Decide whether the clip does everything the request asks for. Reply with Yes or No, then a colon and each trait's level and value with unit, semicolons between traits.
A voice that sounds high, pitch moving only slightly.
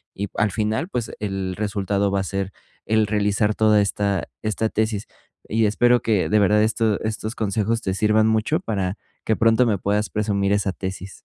No: low, 105 Hz; narrow, 1.8 semitones